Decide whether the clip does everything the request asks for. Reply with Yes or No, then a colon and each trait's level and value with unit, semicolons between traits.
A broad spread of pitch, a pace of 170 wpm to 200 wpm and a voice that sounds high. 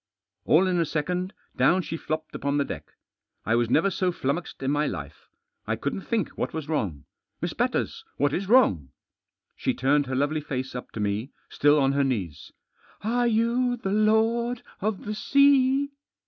No: wide, 8.2 semitones; average, 190 wpm; medium, 160 Hz